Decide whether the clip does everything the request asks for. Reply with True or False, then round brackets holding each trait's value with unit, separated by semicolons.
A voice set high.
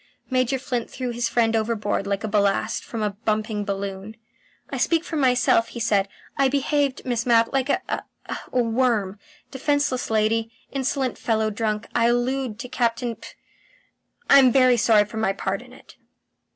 True (230 Hz)